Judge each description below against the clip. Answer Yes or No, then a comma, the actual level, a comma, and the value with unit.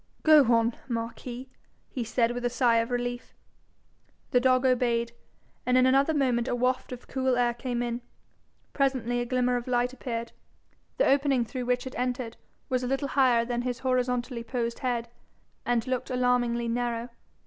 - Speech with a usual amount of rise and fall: No, narrow, 1.3 semitones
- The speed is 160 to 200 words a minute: Yes, average, 170 wpm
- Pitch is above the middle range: Yes, high, 245 Hz